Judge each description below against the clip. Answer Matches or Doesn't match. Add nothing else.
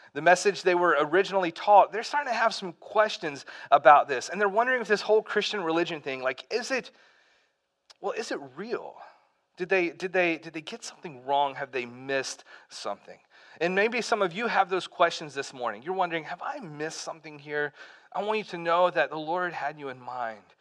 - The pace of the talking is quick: Matches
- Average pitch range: Doesn't match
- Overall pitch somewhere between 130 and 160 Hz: Doesn't match